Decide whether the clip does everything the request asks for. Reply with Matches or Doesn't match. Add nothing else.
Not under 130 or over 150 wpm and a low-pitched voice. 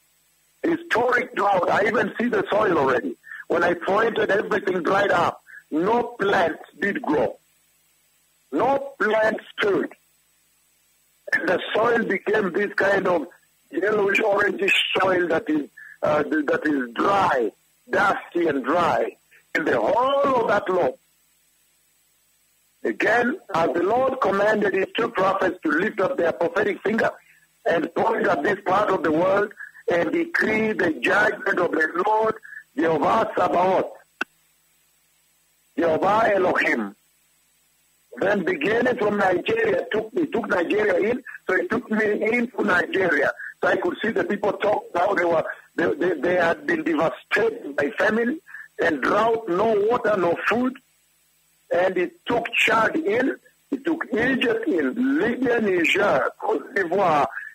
Doesn't match